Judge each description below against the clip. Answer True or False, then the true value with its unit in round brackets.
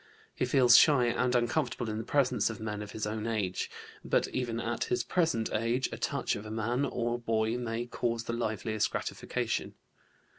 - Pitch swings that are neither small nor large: False (2.0 semitones)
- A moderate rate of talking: True (185 wpm)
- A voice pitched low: True (115 Hz)